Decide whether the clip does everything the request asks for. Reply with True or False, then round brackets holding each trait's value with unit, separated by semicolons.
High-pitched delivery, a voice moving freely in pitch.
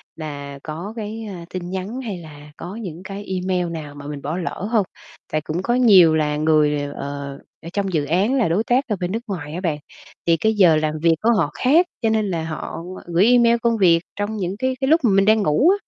False (180 Hz; 5.8 semitones)